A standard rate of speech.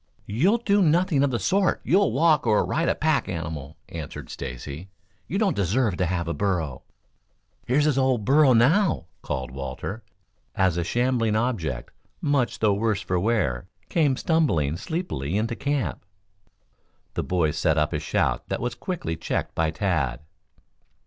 Yes: average, 155 wpm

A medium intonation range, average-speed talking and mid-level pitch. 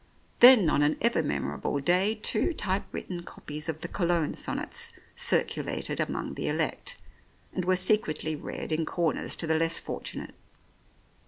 Yes: average, 3.4 semitones; average, 150 wpm; medium, 170 Hz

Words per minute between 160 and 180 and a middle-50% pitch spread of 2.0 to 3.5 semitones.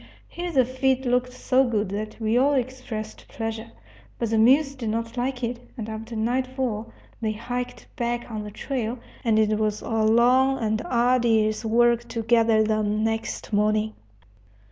Yes: average, 165 wpm; narrow, 2.4 semitones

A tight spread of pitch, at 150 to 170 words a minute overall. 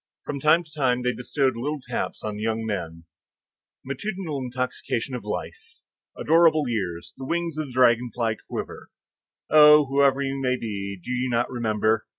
No: average, 4.2 semitones; average, 165 wpm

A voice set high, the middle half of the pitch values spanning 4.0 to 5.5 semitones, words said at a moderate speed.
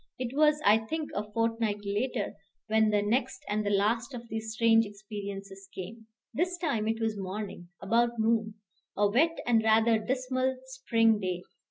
No: high, 225 Hz; average, 2.7 semitones; average, 160 wpm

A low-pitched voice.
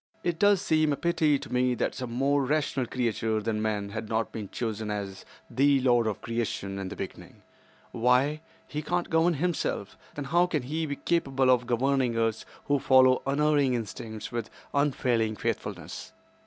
Yes: low, 130 Hz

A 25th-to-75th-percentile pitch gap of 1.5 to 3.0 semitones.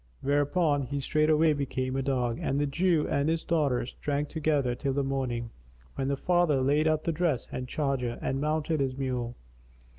Yes: average, 2.7 semitones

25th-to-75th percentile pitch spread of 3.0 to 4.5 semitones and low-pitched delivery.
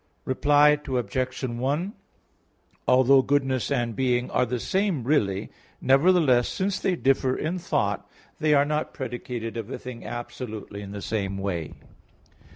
Yes: average, 4.0 semitones; low, 130 Hz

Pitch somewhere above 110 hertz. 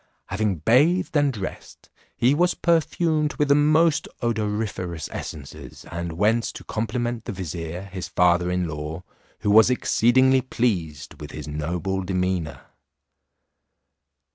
No: low, 105 Hz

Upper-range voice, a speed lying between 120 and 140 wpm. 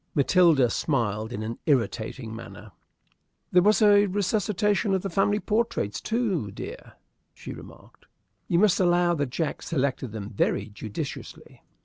No: medium, 165 Hz; slow, 135 wpm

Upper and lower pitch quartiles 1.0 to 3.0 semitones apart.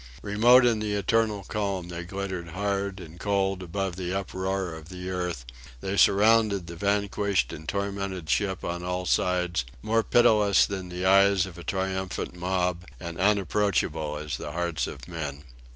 Yes: narrow, 2.4 semitones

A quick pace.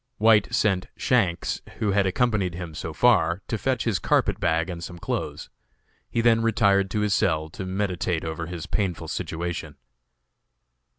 No: average, 160 wpm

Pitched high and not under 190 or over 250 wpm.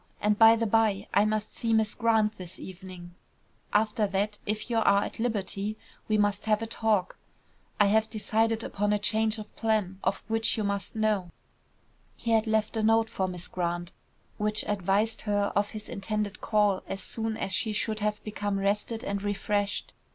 No: high, 210 Hz; average, 180 wpm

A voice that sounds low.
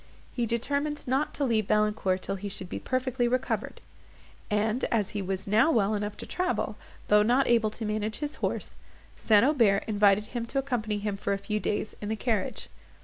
No: high, 215 Hz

